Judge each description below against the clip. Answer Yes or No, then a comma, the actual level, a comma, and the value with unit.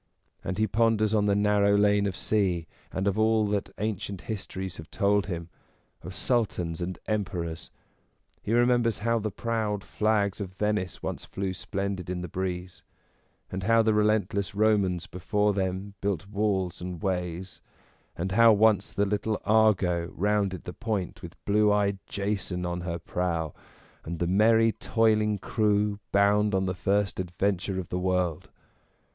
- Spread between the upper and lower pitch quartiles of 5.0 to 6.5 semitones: No, narrow, 2.5 semitones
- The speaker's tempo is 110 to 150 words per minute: No, average, 160 wpm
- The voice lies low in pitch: Yes, low, 100 Hz